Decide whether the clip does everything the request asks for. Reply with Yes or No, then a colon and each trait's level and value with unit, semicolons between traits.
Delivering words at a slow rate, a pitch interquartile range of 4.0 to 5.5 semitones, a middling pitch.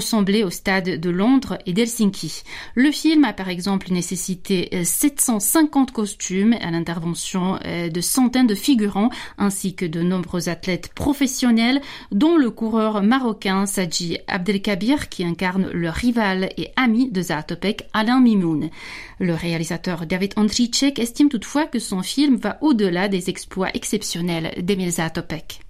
No: slow, 135 wpm; average, 4.9 semitones; high, 200 Hz